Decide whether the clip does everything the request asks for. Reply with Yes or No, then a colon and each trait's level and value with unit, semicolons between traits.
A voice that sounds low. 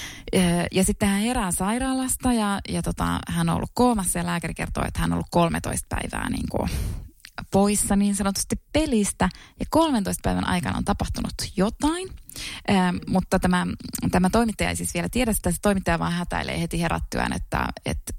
No: medium, 180 Hz